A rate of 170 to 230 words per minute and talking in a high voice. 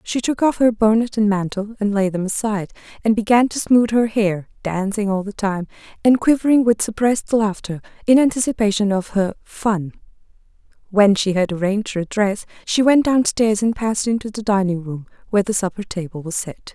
Yes: average, 190 wpm; high, 210 Hz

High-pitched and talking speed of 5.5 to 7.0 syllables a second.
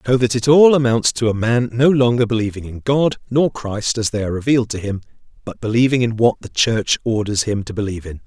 No: low, 115 Hz; 5.9 syllables/s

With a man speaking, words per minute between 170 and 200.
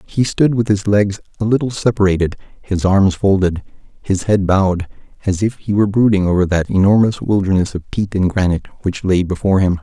Yes: male; average, 190 wpm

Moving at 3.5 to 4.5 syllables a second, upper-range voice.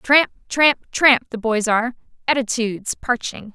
Yes: 4.2 syllables/s; high, 240 Hz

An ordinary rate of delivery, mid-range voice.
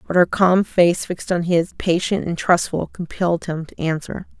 Yes: average, 190 wpm; medium, 175 Hz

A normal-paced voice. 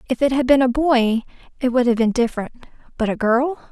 No: fast, 210 wpm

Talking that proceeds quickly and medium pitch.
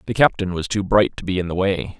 No: fast, 300 wpm; very low, 95 Hz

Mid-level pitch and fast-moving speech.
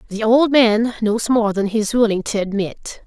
No: high, 220 Hz; fast, 215 wpm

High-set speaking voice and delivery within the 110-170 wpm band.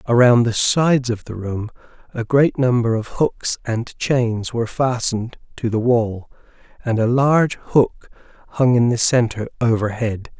No: low, 120 Hz; average, 155 wpm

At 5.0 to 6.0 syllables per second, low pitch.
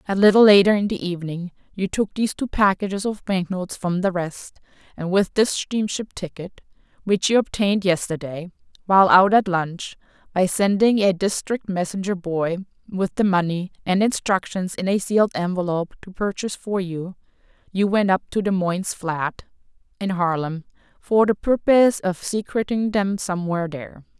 No: 5.2 syllables/s; high, 190 Hz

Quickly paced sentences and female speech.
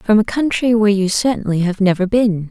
Yes: fast, 215 wpm; female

